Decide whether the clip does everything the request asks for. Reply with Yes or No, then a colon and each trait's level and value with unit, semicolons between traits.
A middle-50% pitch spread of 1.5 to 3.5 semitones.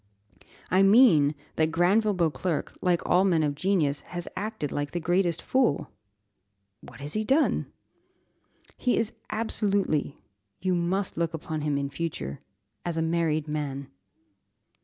No: average, 4.4 semitones